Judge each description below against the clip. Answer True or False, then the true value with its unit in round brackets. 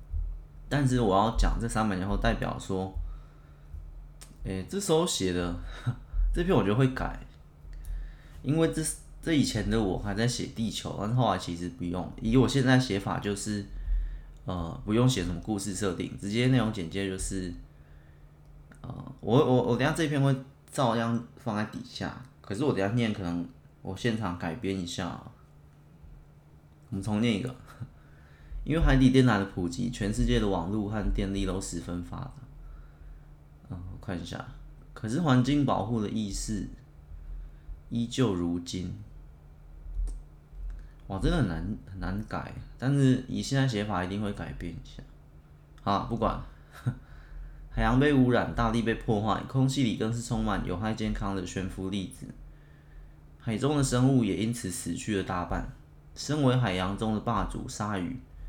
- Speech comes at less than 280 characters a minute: True (235 characters per minute)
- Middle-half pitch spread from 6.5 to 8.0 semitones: True (7.5 semitones)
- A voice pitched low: True (100 Hz)